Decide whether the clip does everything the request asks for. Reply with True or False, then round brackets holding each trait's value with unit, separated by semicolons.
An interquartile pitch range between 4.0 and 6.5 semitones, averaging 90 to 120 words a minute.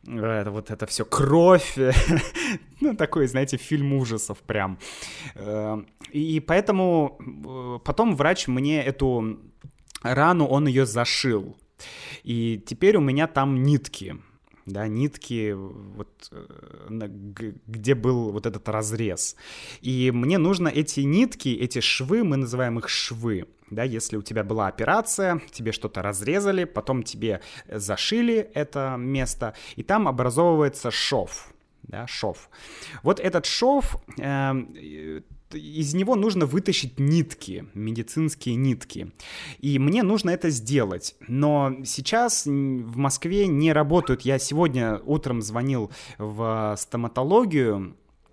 True (5.3 semitones; 115 wpm)